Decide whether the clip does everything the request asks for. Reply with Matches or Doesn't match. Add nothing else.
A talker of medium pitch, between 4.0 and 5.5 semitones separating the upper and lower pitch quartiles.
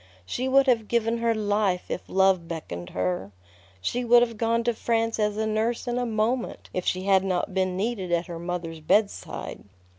Doesn't match